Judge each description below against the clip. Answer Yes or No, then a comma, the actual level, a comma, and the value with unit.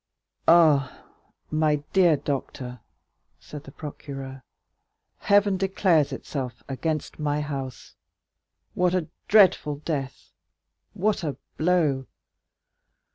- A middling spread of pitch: Yes, average, 4.4 semitones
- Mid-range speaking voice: Yes, medium, 150 Hz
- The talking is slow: Yes, slow, 85 wpm